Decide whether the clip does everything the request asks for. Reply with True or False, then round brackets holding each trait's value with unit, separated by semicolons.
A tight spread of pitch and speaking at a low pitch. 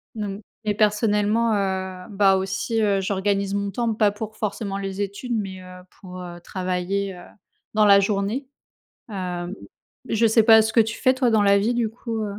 False (2.3 semitones; 200 Hz)